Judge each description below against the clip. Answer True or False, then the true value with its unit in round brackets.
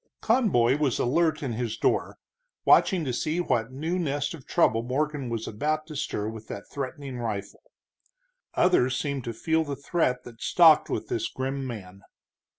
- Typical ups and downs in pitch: True (4.7 semitones)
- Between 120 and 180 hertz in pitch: True (135 Hz)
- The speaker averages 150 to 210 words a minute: True (165 wpm)